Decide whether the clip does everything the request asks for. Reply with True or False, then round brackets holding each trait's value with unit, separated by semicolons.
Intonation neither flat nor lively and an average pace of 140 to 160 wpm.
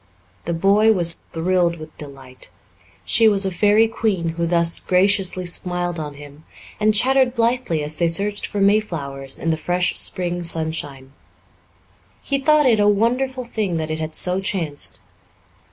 True (4.7 semitones; 155 wpm)